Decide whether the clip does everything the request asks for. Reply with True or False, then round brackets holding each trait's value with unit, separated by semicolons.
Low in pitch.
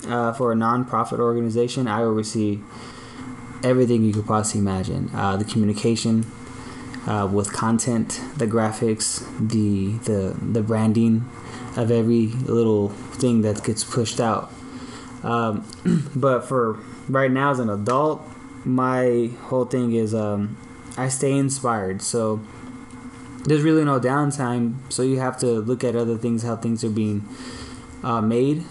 True (120 Hz)